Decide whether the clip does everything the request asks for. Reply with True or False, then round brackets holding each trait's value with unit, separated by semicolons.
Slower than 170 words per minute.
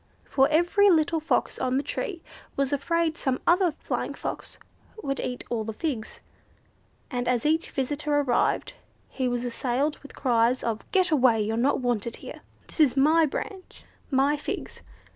True (160 wpm)